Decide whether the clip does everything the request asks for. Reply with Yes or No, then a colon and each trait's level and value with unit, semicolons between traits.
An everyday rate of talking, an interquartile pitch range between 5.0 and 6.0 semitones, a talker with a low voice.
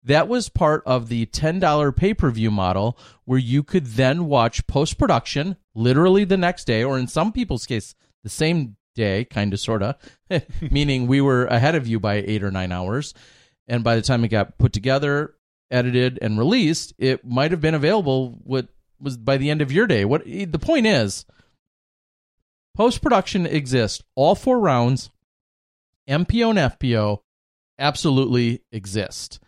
Yes: average, 170 wpm; wide, 5.6 semitones; low, 130 Hz